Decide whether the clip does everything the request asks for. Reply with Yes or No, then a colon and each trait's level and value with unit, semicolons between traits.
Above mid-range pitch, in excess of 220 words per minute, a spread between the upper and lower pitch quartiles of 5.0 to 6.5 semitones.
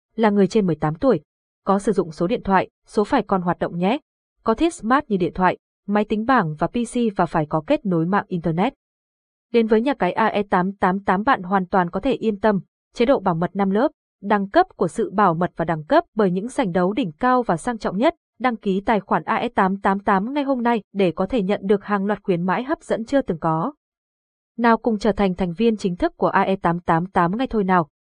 No: high, 205 Hz; average, 230 wpm; average, 4.2 semitones